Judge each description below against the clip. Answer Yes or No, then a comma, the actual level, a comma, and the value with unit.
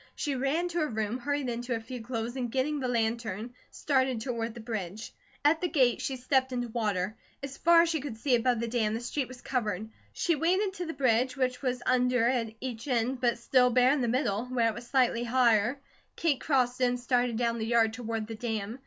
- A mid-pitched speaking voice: No, high, 245 Hz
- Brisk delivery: Yes, fast, 225 wpm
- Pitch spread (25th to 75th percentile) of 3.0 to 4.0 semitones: No, narrow, 2.6 semitones